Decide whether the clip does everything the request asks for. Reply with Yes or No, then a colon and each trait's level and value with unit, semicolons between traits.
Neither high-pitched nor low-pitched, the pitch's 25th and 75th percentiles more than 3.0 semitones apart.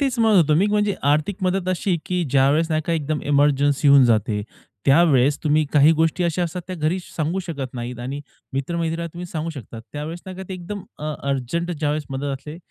Yes: medium, 155 Hz; average, 3.9 semitones